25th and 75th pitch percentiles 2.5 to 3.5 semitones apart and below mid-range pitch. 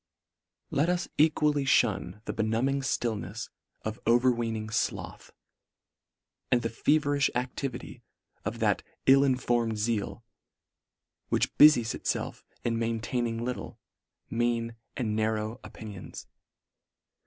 Yes: average, 2.9 semitones; low, 120 Hz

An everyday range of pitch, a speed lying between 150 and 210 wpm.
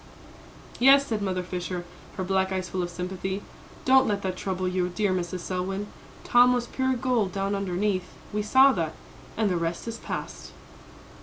Yes: average, 3.2 semitones; average, 170 wpm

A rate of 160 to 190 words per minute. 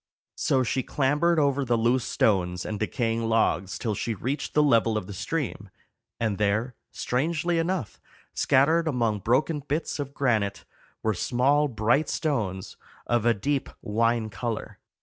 No: average, 150 wpm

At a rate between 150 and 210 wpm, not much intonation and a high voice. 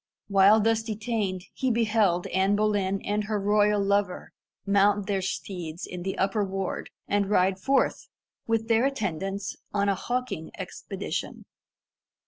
No: slow, 135 wpm; narrow, 2.1 semitones; high, 200 Hz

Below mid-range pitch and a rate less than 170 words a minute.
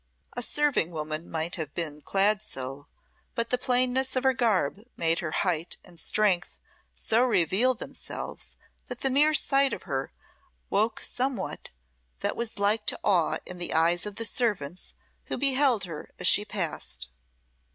No: high, 200 Hz; average, 160 wpm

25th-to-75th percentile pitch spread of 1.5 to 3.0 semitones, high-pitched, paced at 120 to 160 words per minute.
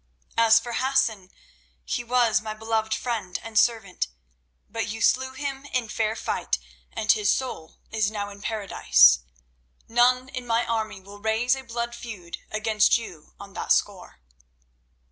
Yes: average, 2.7 semitones; high, 220 Hz; average, 150 wpm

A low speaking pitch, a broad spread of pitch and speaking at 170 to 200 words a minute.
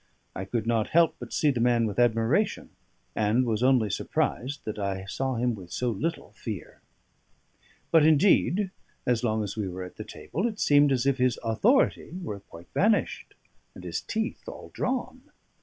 Yes: low, 120 Hz; wide, 6.3 semitones; average, 175 wpm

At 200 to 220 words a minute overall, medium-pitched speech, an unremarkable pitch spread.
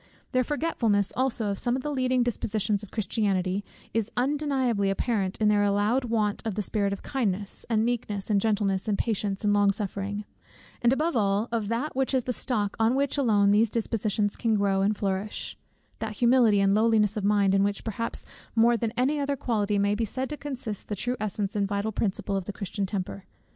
No: fast, 205 wpm; high, 215 Hz; average, 3.1 semitones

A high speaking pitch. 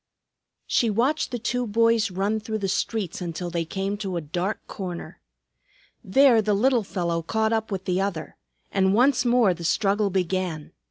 Yes: high, 200 Hz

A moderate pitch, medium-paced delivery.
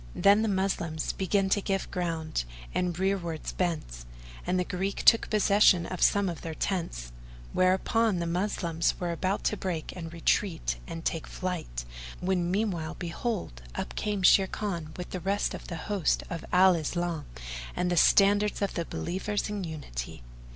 Yes: medium, 180 Hz; average, 160 wpm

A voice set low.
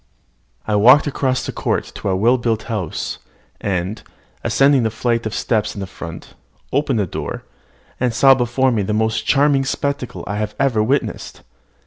Yes: low, 115 Hz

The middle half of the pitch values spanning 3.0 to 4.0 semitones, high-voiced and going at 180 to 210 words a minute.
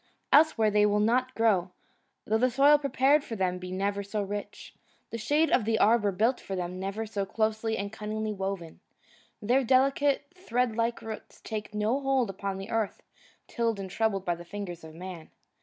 Yes: average, 3.7 semitones; high, 215 Hz; average, 185 wpm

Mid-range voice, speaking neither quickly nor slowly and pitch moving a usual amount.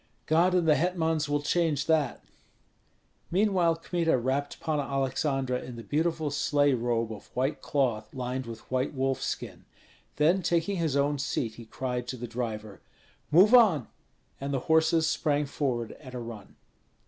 Yes: medium, 145 Hz; average, 155 wpm; average, 4.3 semitones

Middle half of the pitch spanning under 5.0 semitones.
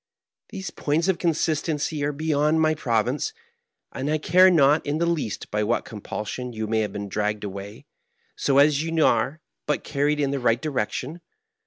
No: wide, 5.5 semitones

